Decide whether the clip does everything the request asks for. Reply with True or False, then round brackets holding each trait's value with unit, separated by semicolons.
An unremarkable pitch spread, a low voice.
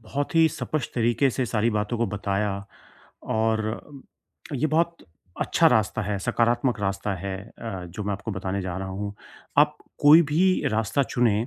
True (4.3 semitones; 110 Hz)